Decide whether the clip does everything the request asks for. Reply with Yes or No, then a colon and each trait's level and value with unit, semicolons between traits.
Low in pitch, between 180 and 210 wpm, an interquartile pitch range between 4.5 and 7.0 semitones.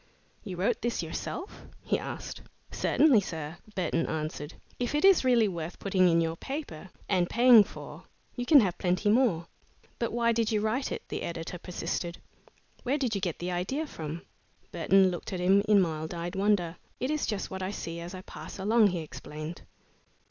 No: high, 190 Hz; average, 185 wpm; average, 5.3 semitones